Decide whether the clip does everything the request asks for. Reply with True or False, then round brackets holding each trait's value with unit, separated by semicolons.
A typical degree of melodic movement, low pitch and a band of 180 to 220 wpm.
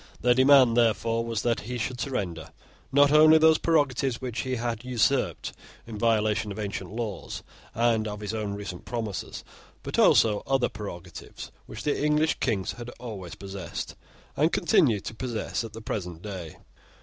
False (3.8 semitones; 115 Hz; 160 wpm)